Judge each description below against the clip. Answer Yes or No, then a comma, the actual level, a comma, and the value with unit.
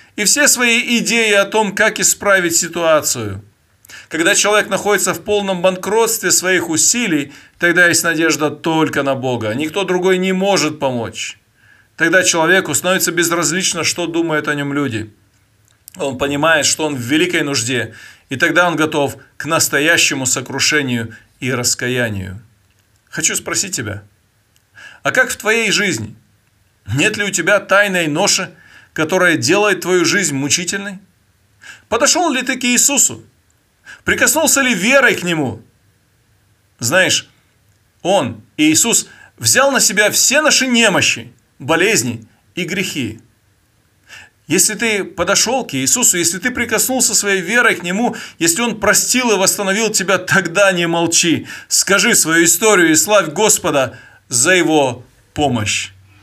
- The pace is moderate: Yes, average, 135 wpm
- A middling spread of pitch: No, wide, 8.0 semitones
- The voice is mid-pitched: Yes, medium, 170 Hz